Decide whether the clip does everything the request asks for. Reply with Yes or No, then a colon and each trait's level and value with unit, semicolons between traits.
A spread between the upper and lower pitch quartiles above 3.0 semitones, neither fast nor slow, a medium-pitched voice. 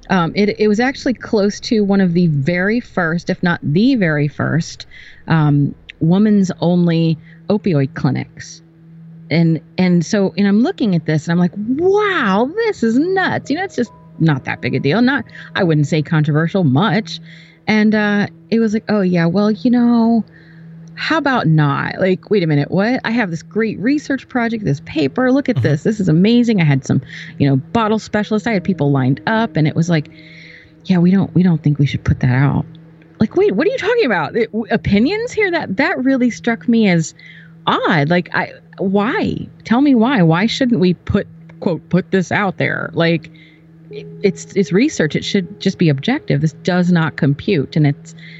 Yes: wide, 5.6 semitones; average, 195 wpm; medium, 180 Hz